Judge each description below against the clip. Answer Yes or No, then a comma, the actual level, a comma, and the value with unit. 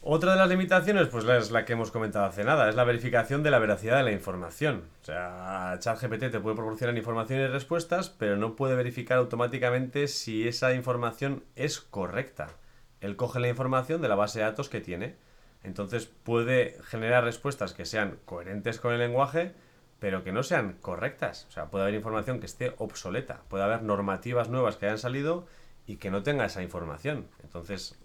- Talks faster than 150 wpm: Yes, fast, 190 wpm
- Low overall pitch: Yes, low, 120 Hz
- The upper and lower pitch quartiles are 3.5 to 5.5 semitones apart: Yes, average, 4.2 semitones